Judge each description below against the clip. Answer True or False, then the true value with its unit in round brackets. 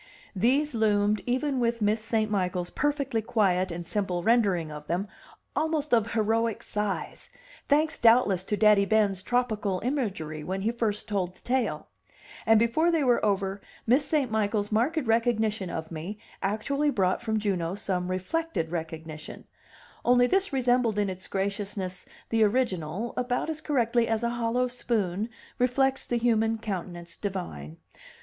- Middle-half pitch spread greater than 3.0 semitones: True (4.3 semitones)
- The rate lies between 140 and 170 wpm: True (150 wpm)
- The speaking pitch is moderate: False (215 Hz)